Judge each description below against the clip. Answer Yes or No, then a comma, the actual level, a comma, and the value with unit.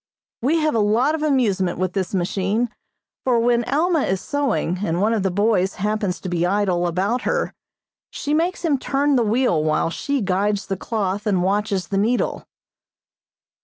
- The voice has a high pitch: Yes, high, 210 Hz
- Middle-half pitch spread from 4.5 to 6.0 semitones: Yes, average, 5.1 semitones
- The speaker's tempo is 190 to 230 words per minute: No, average, 175 wpm